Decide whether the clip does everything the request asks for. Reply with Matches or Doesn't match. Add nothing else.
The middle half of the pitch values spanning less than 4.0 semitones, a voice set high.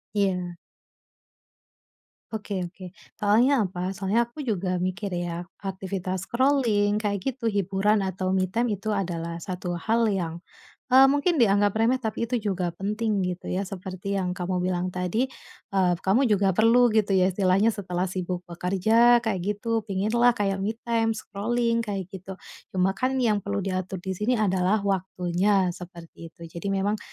Matches